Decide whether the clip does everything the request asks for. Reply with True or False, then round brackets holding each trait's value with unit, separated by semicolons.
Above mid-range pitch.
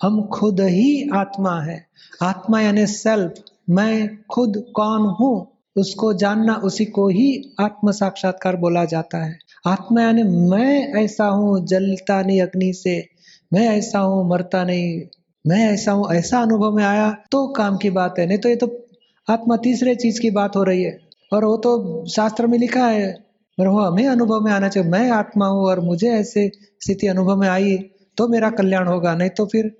True (205 Hz)